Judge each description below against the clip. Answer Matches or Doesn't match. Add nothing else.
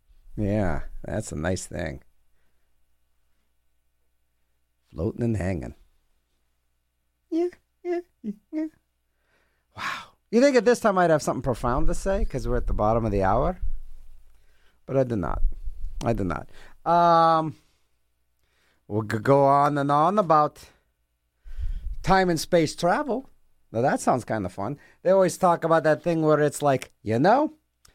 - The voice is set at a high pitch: Doesn't match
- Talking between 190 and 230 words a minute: Doesn't match